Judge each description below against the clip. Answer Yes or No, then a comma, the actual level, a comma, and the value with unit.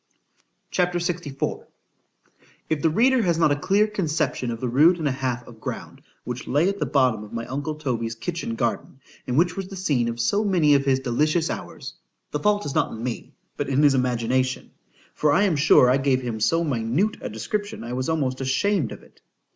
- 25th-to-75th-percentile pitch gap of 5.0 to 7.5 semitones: Yes, wide, 5.5 semitones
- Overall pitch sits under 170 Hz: Yes, medium, 140 Hz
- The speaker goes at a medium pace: No, fast, 210 wpm